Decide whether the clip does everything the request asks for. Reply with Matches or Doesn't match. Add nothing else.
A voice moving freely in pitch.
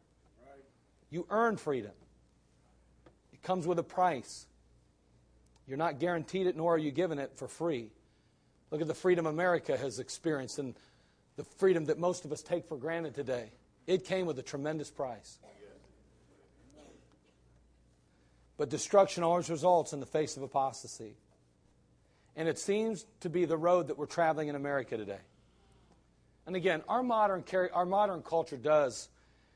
Matches